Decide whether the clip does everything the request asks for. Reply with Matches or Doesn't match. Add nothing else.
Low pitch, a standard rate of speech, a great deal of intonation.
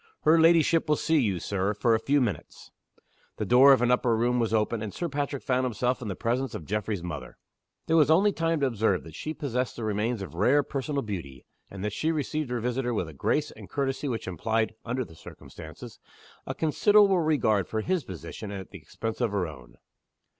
Doesn't match